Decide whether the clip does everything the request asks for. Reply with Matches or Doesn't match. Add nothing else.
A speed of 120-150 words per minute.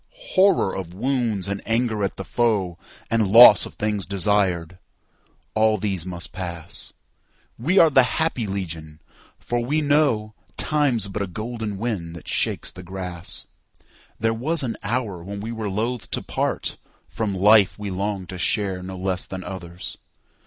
Matches